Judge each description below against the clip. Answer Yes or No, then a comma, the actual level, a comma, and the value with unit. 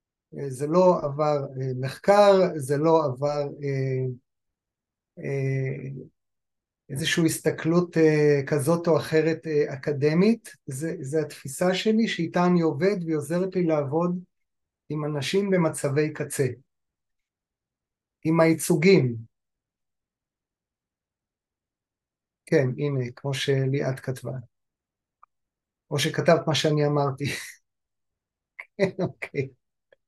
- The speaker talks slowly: Yes, slow, 90 wpm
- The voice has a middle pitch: Yes, medium, 150 Hz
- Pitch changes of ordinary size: Yes, average, 3.5 semitones